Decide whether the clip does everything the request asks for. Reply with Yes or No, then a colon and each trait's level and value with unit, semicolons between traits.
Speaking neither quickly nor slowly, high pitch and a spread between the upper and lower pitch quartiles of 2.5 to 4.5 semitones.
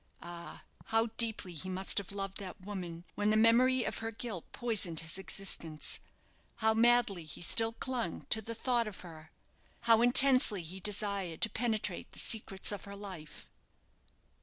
Yes: average, 160 wpm; high, 205 Hz; average, 3.8 semitones